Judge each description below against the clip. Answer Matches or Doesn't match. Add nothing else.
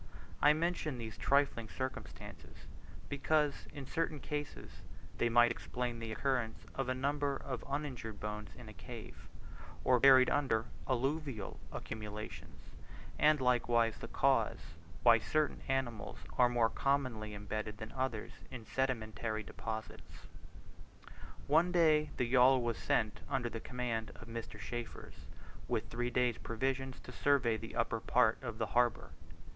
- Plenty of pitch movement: Doesn't match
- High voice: Doesn't match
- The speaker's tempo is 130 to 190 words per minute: Matches